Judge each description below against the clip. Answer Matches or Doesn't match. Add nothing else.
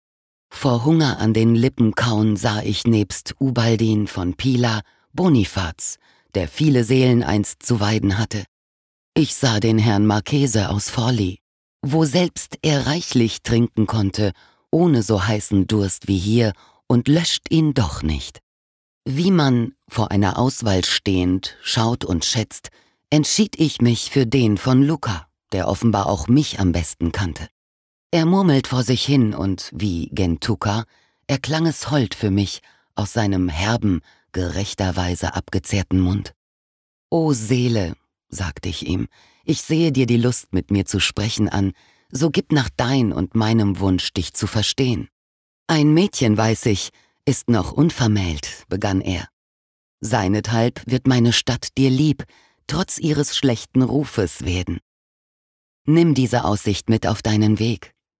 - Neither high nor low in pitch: Doesn't match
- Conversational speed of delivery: Matches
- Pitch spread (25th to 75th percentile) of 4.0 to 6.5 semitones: Matches